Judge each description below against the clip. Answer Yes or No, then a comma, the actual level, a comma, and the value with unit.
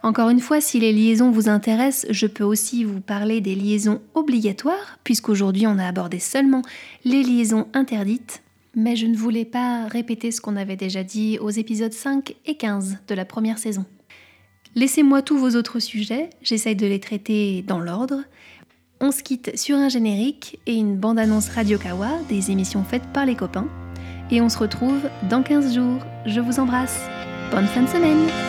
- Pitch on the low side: No, high, 225 Hz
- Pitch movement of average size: Yes, average, 3.6 semitones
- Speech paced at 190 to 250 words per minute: No, average, 180 wpm